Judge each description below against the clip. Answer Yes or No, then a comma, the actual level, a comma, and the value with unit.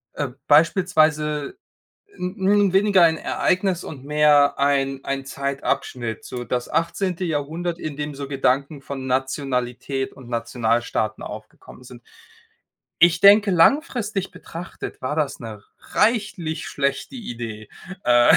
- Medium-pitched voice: Yes, medium, 145 Hz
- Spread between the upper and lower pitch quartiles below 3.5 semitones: No, average, 5.0 semitones